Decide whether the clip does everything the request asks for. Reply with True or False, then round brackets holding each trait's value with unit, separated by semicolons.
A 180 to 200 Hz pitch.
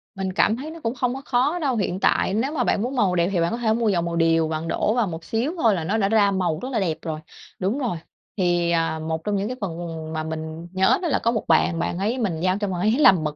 True (195 Hz)